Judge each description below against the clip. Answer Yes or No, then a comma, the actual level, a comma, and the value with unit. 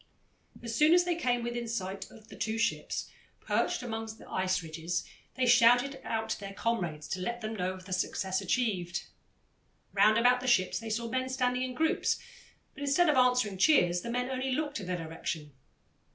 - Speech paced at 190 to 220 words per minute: Yes, average, 195 wpm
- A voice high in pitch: Yes, high, 230 Hz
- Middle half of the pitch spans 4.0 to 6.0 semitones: Yes, average, 5.1 semitones